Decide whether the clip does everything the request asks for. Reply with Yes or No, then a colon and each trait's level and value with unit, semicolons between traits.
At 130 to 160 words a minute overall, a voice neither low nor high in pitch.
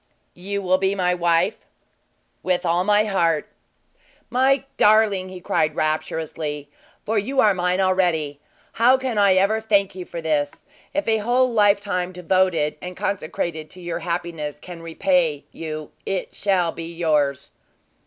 Yes: average, 145 wpm; medium, 180 Hz